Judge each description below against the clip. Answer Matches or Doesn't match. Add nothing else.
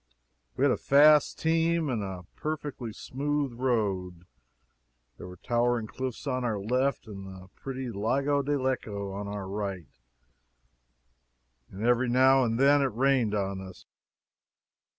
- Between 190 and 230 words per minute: Doesn't match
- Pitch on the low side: Matches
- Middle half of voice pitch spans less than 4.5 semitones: Doesn't match